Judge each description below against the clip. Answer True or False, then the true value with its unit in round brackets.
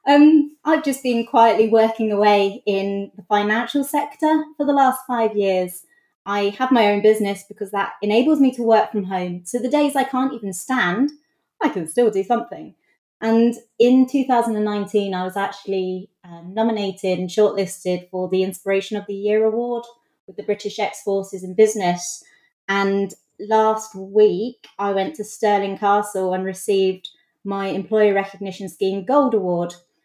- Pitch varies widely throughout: False (3.3 semitones)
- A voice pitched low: False (210 Hz)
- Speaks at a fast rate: False (160 wpm)